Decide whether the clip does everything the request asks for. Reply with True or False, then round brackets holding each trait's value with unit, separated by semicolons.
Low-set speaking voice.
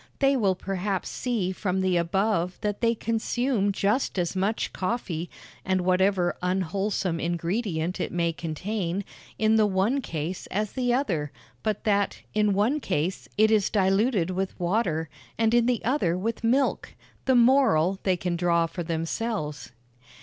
False (195 Hz)